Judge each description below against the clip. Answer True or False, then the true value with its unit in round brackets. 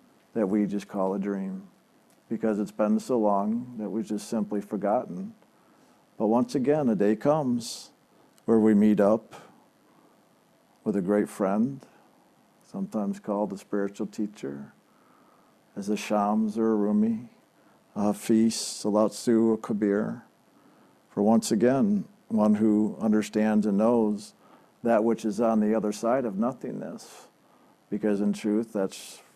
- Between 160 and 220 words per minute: False (140 wpm)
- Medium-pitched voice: False (110 Hz)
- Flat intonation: True (1.8 semitones)